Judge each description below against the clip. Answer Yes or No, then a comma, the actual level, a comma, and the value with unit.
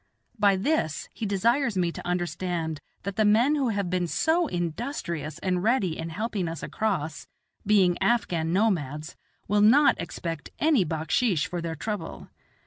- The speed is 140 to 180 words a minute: Yes, average, 150 wpm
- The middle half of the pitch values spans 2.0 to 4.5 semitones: No, average, 4.9 semitones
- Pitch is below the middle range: No, medium, 185 Hz